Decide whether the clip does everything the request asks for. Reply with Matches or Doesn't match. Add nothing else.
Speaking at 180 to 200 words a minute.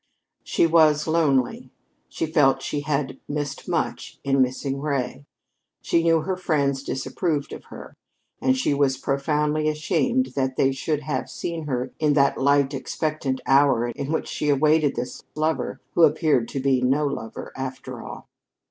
Doesn't match